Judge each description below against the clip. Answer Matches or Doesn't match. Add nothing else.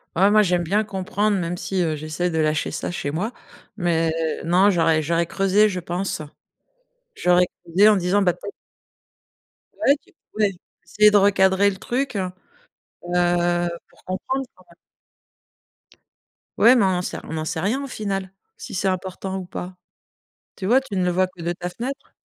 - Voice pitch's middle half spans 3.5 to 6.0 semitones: Doesn't match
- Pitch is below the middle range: Doesn't match